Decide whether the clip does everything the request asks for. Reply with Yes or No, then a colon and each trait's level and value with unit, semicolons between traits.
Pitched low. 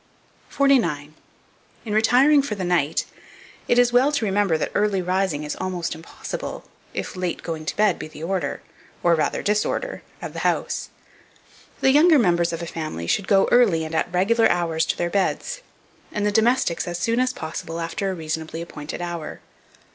No: medium, 185 Hz